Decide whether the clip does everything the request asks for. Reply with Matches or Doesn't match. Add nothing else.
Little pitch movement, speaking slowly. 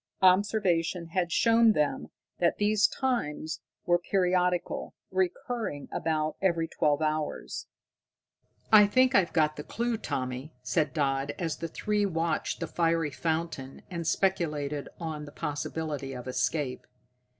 Doesn't match